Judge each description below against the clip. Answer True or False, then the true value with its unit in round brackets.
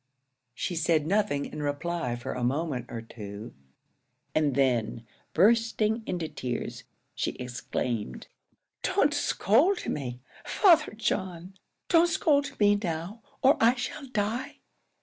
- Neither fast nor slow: False (120 wpm)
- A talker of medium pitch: True (170 Hz)